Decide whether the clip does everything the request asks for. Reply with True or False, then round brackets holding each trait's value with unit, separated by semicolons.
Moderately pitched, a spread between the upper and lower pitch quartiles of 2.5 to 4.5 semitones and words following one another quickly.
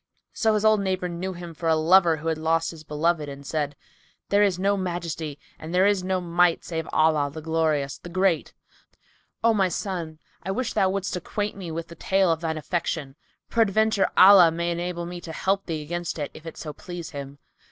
True (170 Hz; 3.0 semitones; 210 wpm)